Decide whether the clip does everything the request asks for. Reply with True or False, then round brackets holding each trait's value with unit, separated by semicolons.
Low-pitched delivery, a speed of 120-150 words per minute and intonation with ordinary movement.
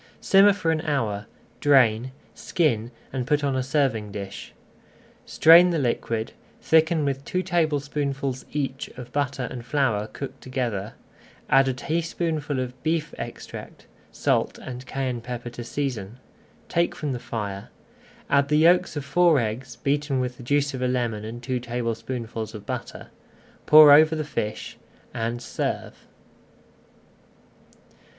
True (130 Hz; 140 wpm; 3.9 semitones)